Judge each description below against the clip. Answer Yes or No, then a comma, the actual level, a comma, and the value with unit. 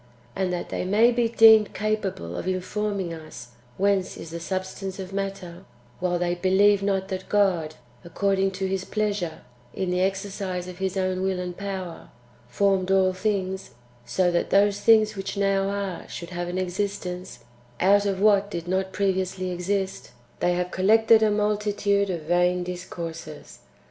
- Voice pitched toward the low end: No, high, 190 Hz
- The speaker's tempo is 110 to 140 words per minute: No, average, 160 wpm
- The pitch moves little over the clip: Yes, narrow, 1.9 semitones